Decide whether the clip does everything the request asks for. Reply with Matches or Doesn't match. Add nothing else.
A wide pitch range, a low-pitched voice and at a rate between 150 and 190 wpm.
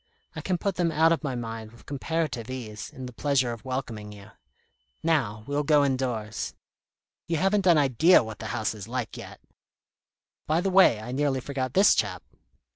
Matches